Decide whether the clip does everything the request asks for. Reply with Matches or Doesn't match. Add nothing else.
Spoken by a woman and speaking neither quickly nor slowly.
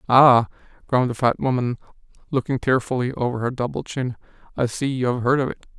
Doesn't match